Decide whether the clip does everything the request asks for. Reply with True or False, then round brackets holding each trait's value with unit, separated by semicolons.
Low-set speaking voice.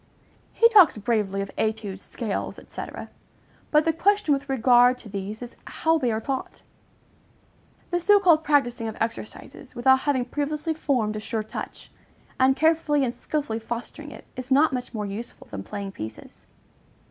False (250 Hz)